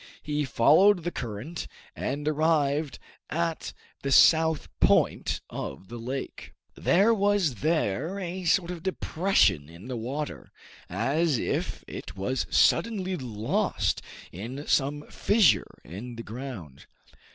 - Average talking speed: No, slow, 120 wpm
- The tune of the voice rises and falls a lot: Yes, wide, 6.3 semitones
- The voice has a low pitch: No, medium, 145 Hz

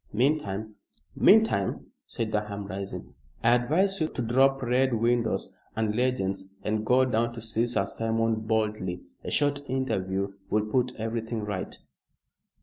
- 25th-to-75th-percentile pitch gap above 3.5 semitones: No, average, 3.1 semitones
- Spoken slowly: No, average, 145 wpm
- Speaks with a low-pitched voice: Yes, low, 115 Hz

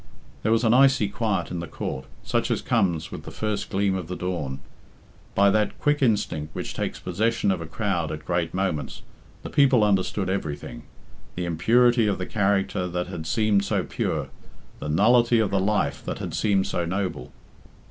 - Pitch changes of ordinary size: Yes, average, 3.8 semitones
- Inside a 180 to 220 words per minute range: Yes, average, 185 wpm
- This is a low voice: Yes, very low, 95 Hz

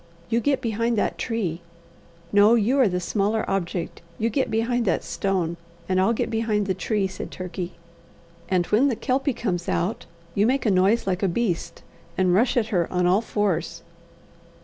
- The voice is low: No, high, 205 Hz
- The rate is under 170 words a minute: No, average, 180 wpm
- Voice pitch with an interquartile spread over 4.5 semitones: No, average, 3.9 semitones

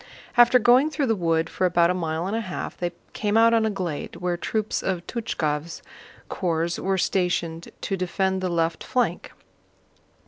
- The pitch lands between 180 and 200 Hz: Yes, medium, 185 Hz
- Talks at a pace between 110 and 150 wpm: No, average, 175 wpm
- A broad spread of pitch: No, average, 4.3 semitones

